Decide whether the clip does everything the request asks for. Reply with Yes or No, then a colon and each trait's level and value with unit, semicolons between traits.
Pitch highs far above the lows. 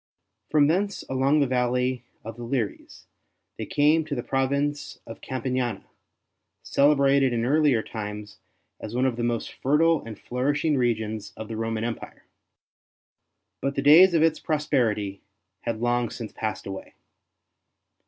No: average, 4.2 semitones